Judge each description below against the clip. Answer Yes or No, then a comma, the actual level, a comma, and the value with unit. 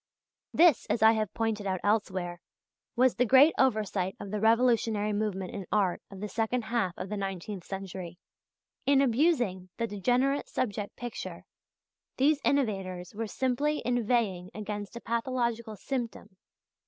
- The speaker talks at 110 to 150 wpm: Yes, average, 140 wpm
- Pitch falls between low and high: No, high, 220 Hz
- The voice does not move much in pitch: No, average, 3.9 semitones